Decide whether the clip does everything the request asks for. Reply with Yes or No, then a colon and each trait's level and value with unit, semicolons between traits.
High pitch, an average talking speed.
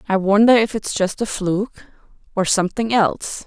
Yes: high, 205 Hz; average, 155 wpm